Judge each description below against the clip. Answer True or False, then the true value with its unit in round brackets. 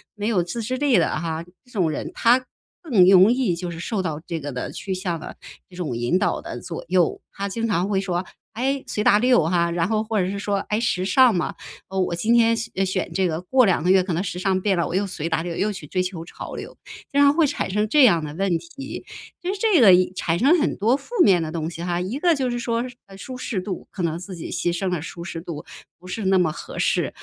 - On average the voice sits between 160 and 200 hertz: True (190 Hz)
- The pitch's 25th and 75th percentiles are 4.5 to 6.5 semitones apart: True (5.0 semitones)